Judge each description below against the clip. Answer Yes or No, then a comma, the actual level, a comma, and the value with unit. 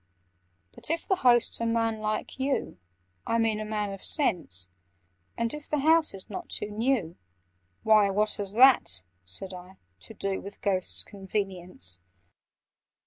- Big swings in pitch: No, average, 3.7 semitones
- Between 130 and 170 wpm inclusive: Yes, average, 150 wpm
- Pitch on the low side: No, high, 210 Hz